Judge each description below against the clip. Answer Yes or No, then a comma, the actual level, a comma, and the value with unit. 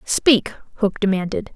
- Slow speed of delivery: Yes, slow, 115 wpm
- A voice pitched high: Yes, high, 205 Hz